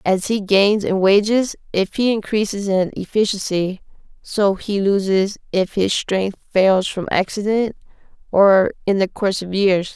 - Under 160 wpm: Yes, average, 150 wpm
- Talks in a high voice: Yes, high, 200 Hz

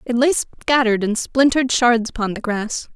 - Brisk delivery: No, average, 180 wpm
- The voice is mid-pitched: No, high, 240 Hz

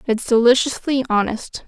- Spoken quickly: No, slow, 105 wpm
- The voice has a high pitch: Yes, high, 240 Hz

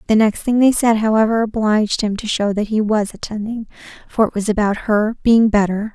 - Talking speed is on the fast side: Yes, fast, 210 wpm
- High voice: Yes, high, 215 Hz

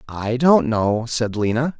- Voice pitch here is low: Yes, low, 120 Hz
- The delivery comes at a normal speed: Yes, average, 165 wpm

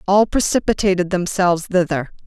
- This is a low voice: No, medium, 185 Hz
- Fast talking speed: No, slow, 105 wpm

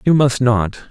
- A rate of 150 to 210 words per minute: Yes, average, 200 wpm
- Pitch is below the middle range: Yes, low, 125 Hz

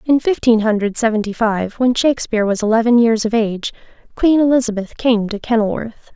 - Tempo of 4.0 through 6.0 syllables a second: Yes, 5.7 syllables/s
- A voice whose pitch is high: Yes, high, 225 Hz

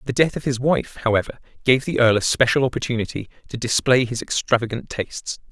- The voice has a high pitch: No, low, 125 Hz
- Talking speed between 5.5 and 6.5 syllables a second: Yes, 6.0 syllables/s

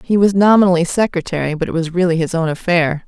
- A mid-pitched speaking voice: Yes, medium, 175 Hz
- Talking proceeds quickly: Yes, fast, 215 wpm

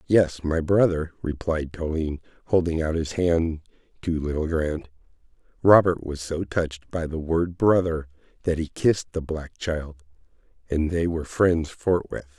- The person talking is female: No, male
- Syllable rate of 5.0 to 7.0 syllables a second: No, 4.5 syllables/s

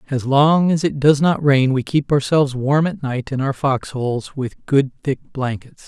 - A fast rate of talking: Yes, fast, 215 wpm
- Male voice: Yes, male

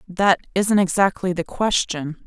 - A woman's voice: Yes, female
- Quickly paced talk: No, slow, 135 wpm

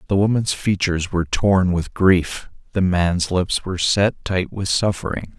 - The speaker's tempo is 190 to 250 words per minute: No, average, 165 wpm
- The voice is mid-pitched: No, very low, 95 Hz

